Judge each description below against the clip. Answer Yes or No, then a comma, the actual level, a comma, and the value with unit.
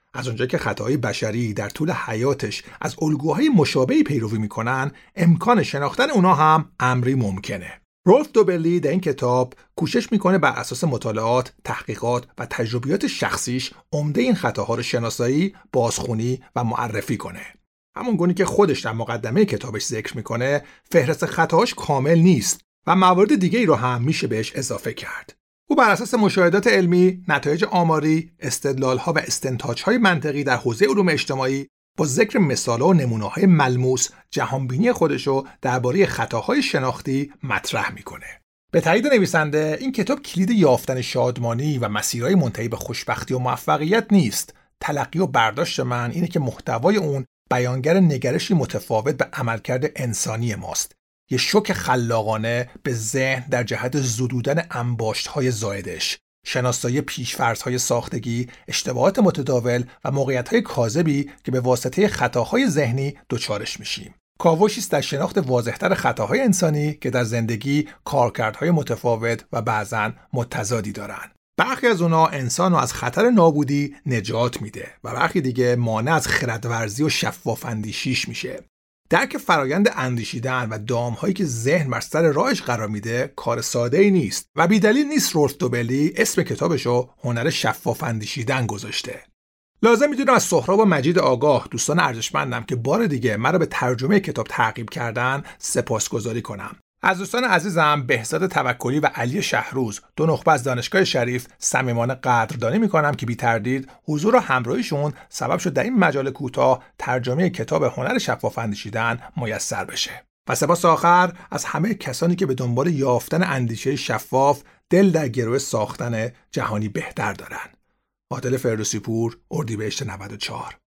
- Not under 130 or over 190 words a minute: Yes, average, 145 wpm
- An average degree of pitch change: No, wide, 5.9 semitones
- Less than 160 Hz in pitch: Yes, low, 135 Hz